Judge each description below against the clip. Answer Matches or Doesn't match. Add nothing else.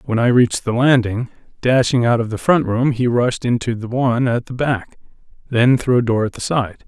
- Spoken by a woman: Doesn't match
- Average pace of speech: Doesn't match